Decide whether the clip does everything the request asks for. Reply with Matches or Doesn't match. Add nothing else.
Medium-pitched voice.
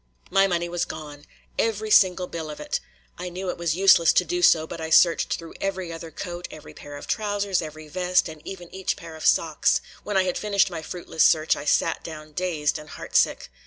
Matches